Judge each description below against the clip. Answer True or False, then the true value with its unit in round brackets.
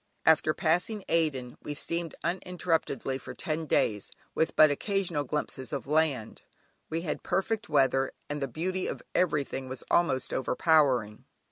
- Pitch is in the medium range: True (155 Hz)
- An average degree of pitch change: True (4.2 semitones)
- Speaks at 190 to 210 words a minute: False (140 wpm)